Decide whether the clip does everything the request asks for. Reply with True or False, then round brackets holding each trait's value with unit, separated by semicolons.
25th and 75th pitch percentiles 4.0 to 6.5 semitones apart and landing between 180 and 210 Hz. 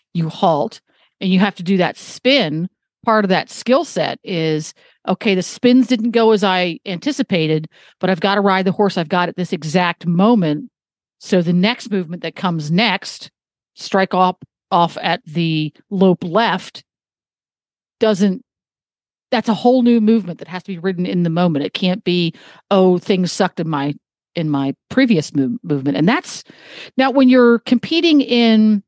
True (4.7 semitones; 190 Hz)